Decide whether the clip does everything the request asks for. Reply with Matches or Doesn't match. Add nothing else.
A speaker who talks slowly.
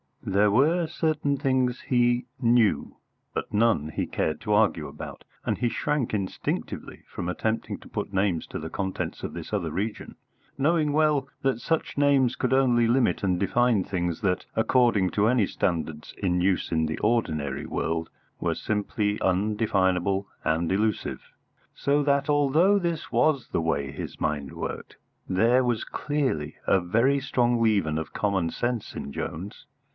Doesn't match